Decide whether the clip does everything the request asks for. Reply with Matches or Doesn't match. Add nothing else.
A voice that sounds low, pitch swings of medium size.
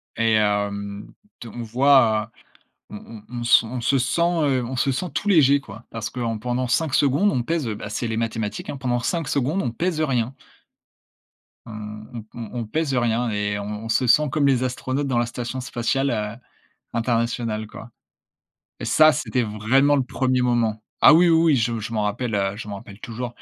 Matches